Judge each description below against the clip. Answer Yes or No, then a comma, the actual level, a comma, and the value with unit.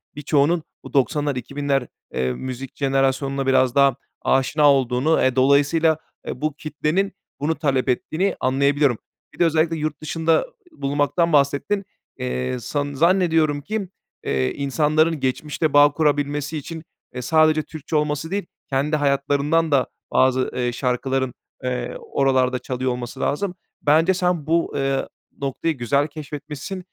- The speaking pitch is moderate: Yes, medium, 145 Hz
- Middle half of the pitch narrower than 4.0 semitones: Yes, average, 2.9 semitones